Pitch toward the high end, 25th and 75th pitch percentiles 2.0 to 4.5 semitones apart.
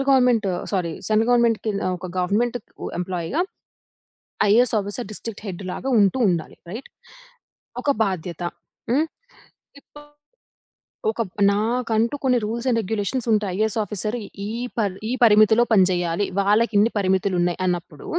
Yes: high, 210 Hz; average, 4.0 semitones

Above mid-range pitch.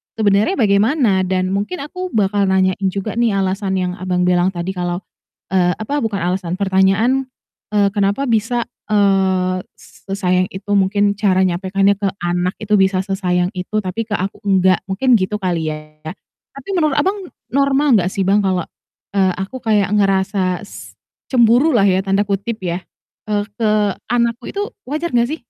Yes: high, 195 Hz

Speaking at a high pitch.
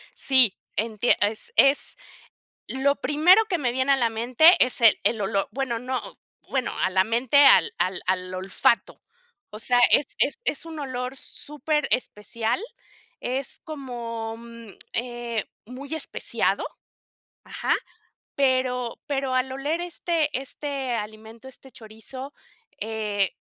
Yes: very high, 250 Hz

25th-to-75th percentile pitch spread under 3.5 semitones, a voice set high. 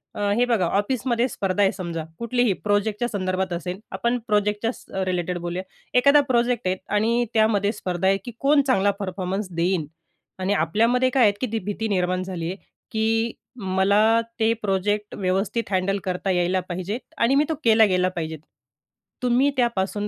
No: average, 3.8 semitones; high, 205 Hz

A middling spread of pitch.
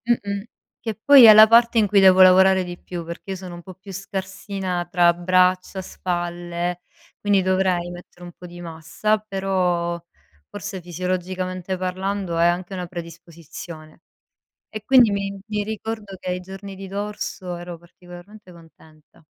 No: narrow, 2.2 semitones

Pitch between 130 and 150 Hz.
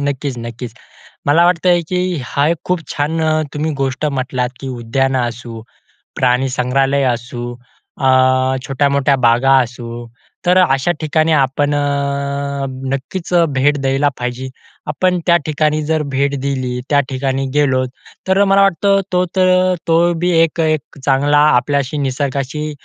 Yes: medium, 140 Hz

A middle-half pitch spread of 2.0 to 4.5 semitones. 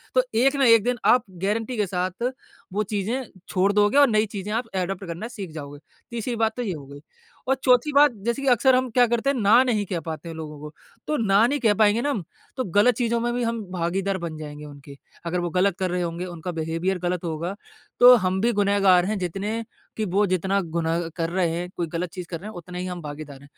No: average, 5.0 semitones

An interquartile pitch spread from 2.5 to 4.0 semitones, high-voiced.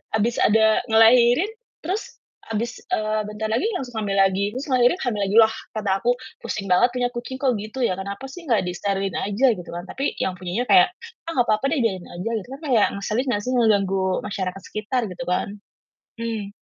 Yes: average, 3.7 semitones; high, 220 Hz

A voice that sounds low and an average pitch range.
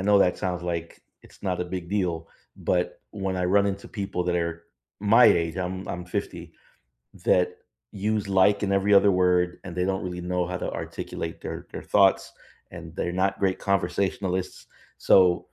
No: very low, 90 Hz; narrow, 1.8 semitones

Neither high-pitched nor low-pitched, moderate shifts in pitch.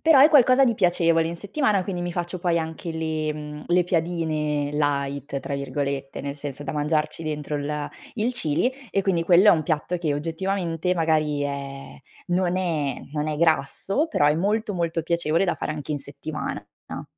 Yes: medium, 160 Hz; average, 3.2 semitones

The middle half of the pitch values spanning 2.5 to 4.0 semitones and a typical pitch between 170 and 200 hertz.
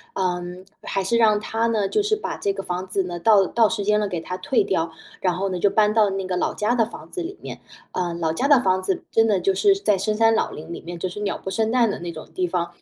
Yes: average, 3.7 semitones; high, 195 Hz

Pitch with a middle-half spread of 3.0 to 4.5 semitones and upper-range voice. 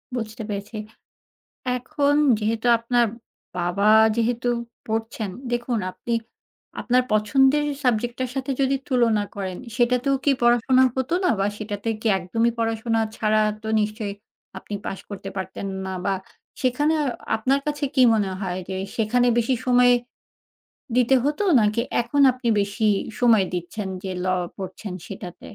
Yes: average, 3.3 semitones; high, 230 Hz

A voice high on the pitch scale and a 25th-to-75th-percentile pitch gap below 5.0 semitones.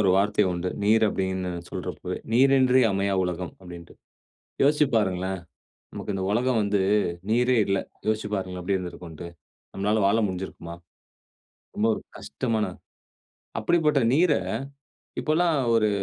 No: low, 100 Hz; average, 4.4 semitones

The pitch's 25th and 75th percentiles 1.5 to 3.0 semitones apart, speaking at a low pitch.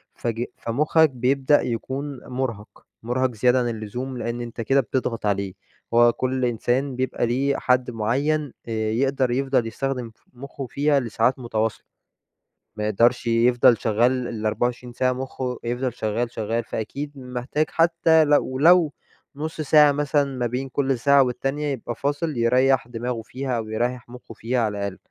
Yes: average, 2.7 semitones; low, 125 Hz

